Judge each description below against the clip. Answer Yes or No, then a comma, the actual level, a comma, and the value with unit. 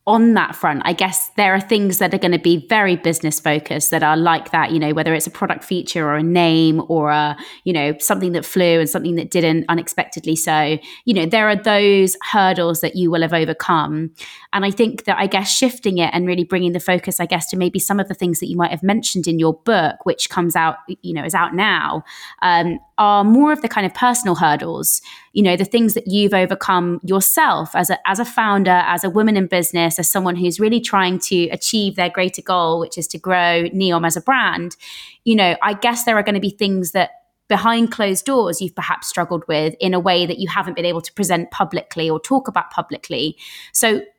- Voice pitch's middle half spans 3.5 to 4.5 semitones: No, average, 3.0 semitones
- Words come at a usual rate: No, fast, 230 wpm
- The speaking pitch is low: No, medium, 180 Hz